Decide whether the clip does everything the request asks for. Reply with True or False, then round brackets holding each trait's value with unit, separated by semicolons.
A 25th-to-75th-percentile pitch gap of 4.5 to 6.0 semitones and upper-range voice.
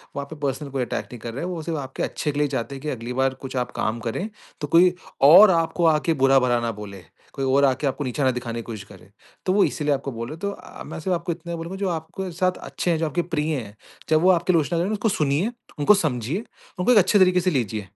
False (5.1 semitones; 150 Hz)